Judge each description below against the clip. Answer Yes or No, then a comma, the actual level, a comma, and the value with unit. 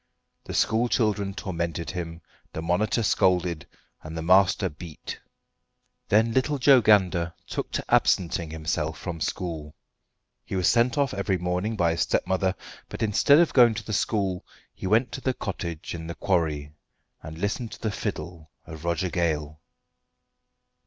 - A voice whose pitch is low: Yes, very low, 90 Hz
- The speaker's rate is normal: Yes, average, 155 wpm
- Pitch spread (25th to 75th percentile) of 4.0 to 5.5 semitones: Yes, average, 4.5 semitones